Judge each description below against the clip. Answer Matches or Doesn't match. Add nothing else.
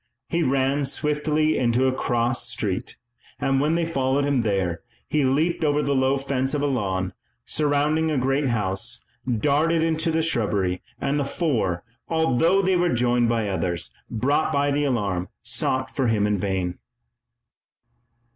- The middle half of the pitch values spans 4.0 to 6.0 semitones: Matches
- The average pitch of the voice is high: Doesn't match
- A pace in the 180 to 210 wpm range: Doesn't match